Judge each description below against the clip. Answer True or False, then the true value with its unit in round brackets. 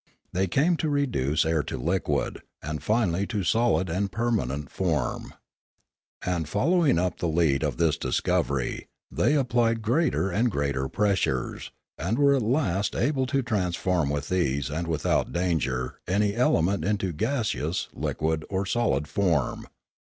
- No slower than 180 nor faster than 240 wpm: False (145 wpm)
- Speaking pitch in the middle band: False (95 Hz)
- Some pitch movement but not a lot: False (6.8 semitones)